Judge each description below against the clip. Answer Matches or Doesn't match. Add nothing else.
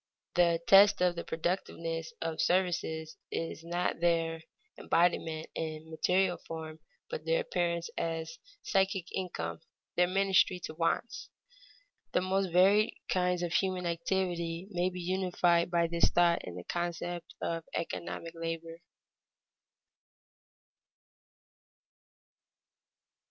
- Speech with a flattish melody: Matches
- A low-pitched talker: Doesn't match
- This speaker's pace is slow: Matches